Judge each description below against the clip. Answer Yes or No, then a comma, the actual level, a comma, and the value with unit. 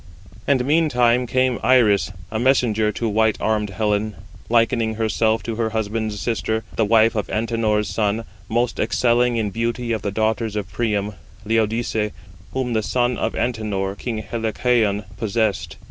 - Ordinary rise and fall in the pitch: No, narrow, 1.9 semitones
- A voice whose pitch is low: Yes, low, 110 Hz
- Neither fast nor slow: Yes, average, 145 wpm